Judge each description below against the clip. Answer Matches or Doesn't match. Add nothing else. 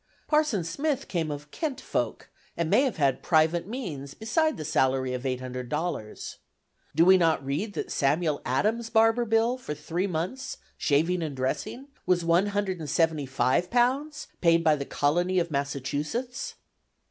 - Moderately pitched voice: Matches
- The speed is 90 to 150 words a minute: Matches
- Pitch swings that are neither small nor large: Doesn't match